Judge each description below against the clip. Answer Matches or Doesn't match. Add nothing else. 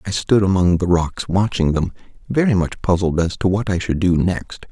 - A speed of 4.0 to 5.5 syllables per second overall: Matches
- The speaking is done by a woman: Doesn't match